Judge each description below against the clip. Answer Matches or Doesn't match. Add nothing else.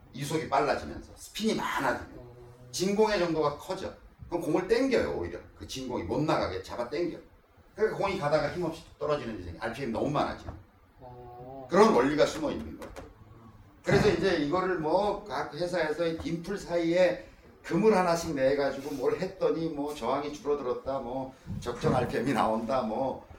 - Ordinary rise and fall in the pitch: Doesn't match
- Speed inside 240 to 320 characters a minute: Doesn't match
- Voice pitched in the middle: Matches